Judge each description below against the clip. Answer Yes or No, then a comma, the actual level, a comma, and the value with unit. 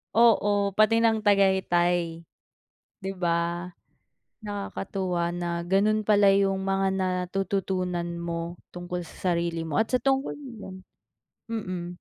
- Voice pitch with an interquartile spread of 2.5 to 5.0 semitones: Yes, average, 2.8 semitones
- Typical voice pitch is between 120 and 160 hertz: No, high, 190 Hz